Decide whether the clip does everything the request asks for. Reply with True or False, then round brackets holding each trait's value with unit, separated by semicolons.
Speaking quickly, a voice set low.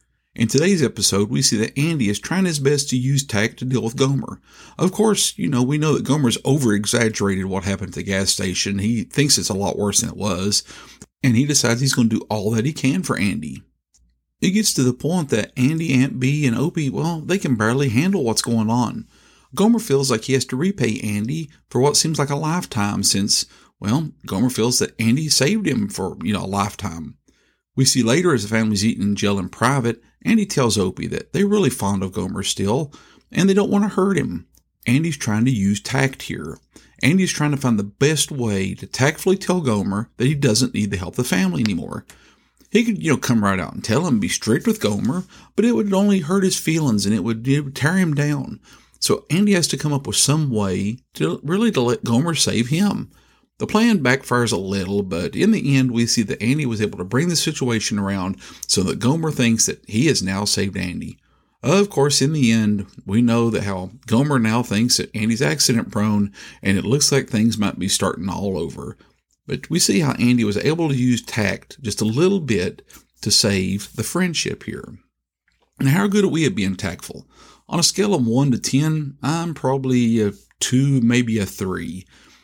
True (215 wpm; 125 Hz)